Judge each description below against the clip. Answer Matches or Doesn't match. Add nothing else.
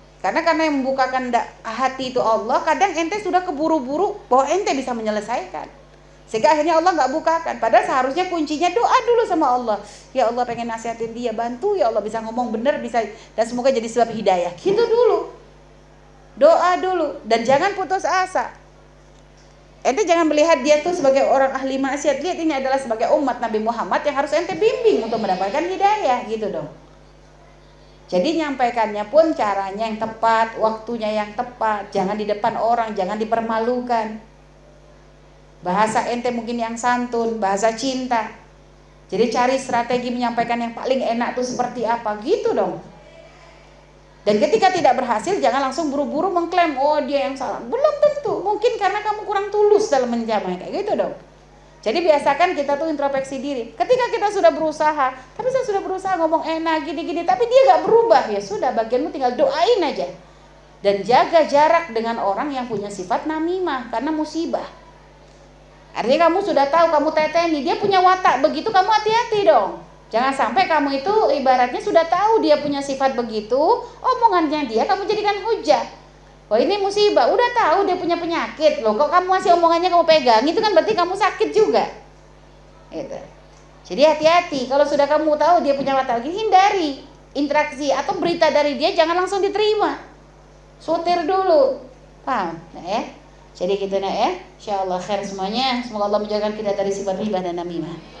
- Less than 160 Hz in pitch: Doesn't match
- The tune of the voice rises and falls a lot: Matches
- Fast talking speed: Matches